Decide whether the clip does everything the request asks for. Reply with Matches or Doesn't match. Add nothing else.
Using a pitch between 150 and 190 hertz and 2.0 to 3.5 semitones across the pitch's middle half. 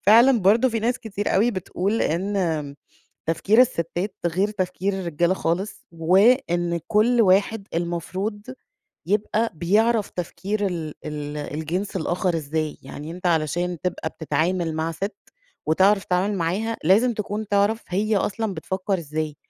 Doesn't match